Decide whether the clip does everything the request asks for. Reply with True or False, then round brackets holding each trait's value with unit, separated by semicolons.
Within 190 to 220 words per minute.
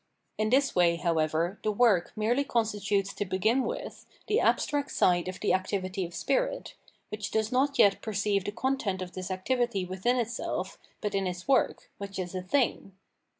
False (180 wpm)